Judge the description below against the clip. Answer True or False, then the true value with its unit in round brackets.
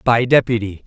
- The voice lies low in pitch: True (115 Hz)